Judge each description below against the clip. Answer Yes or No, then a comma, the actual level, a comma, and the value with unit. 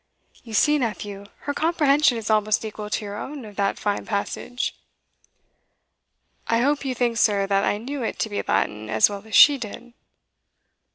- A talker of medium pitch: No, high, 220 Hz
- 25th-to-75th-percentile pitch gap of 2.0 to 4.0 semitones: No, average, 4.4 semitones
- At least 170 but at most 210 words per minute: Yes, average, 175 wpm